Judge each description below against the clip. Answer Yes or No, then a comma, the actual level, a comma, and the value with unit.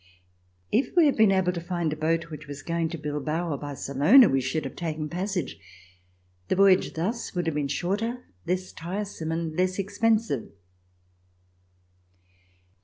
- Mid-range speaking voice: Yes, medium, 170 Hz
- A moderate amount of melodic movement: Yes, average, 4.2 semitones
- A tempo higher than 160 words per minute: No, average, 155 wpm